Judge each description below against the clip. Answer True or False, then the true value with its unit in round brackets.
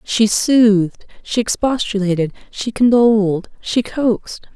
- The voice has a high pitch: True (215 Hz)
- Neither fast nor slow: False (105 wpm)